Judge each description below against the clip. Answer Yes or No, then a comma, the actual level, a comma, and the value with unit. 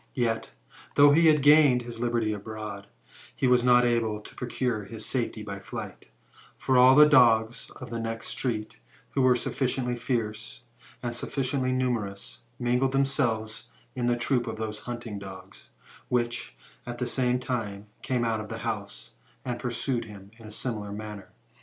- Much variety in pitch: No, narrow, 2.6 semitones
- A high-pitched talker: No, low, 120 Hz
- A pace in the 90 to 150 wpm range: No, average, 165 wpm